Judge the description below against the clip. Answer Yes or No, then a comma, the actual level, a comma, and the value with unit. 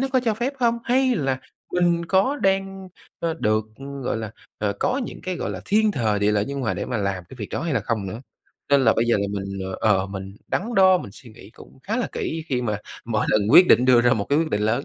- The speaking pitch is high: No, low, 130 Hz